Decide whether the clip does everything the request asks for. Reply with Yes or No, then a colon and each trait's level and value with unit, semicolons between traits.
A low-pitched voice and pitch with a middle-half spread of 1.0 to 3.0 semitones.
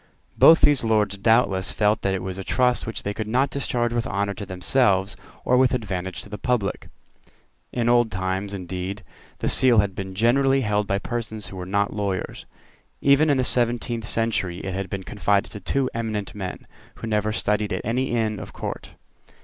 No: low, 105 Hz; average, 3.5 semitones